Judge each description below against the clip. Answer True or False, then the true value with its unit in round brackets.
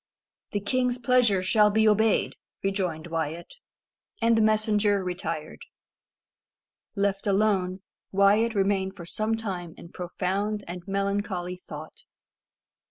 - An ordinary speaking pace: False (110 wpm)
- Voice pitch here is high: True (200 Hz)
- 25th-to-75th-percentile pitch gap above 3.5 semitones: False (3.0 semitones)